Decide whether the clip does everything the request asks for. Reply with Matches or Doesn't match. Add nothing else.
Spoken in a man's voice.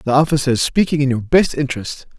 Matches